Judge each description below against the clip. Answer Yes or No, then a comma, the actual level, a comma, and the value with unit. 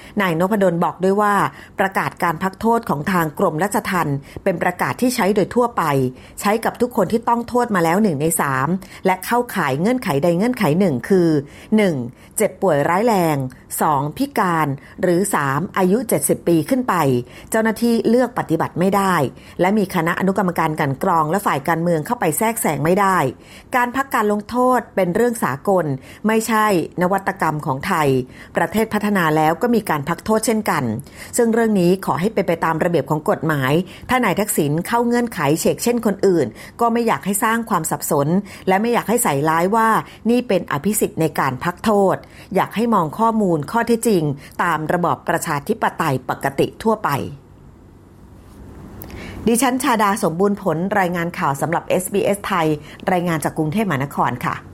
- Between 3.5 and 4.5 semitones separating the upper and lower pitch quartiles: No, average, 5.3 semitones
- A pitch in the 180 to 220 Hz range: Yes, medium, 185 Hz